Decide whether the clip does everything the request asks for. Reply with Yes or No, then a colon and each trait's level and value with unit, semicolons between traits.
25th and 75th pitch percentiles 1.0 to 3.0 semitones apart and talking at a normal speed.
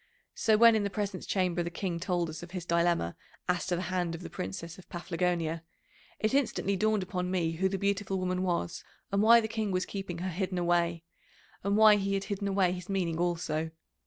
No: narrow, 2.5 semitones; fast, 215 wpm